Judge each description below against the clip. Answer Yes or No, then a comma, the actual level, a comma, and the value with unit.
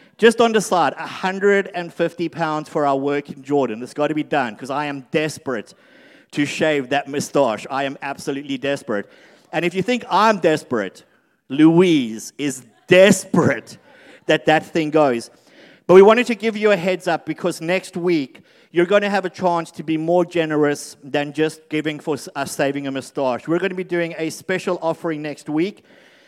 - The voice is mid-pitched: Yes, medium, 160 Hz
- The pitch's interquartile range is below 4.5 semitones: Yes, average, 4.1 semitones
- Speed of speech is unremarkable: Yes, average, 185 wpm